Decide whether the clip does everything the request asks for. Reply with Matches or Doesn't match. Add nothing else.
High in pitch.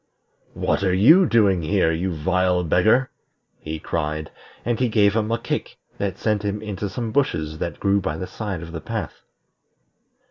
Doesn't match